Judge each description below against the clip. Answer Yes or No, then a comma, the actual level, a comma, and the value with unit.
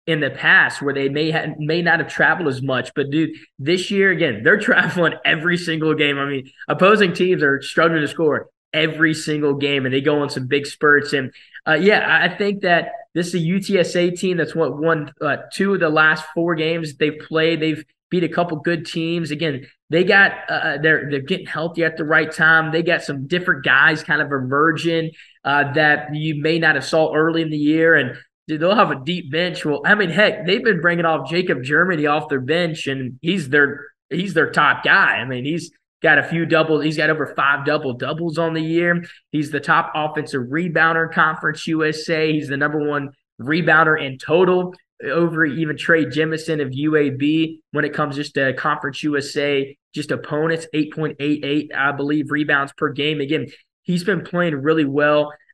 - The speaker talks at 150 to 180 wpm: No, average, 200 wpm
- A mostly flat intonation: Yes, narrow, 2.2 semitones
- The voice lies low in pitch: No, medium, 155 Hz